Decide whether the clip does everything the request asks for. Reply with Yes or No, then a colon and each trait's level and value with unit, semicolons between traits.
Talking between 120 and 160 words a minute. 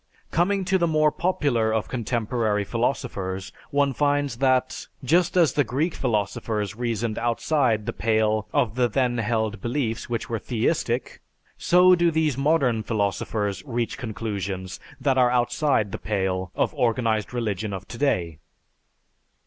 Yes: average, 140 wpm